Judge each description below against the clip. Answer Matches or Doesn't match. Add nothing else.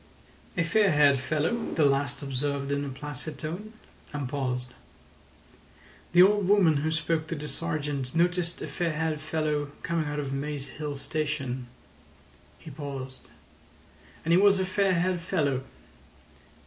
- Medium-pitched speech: Matches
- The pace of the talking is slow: Doesn't match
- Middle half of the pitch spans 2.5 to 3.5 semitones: Matches